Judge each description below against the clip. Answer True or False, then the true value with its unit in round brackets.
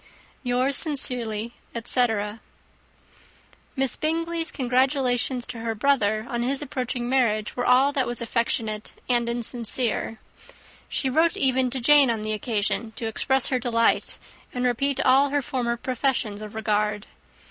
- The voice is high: True (245 Hz)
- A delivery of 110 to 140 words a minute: True (135 wpm)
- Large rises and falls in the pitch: False (2.9 semitones)